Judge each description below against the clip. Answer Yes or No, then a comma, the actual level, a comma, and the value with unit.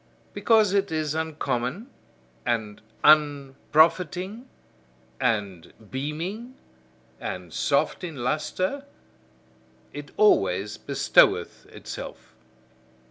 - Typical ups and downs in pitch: No, wide, 7.1 semitones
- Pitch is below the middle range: No, medium, 155 Hz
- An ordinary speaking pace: No, slow, 75 wpm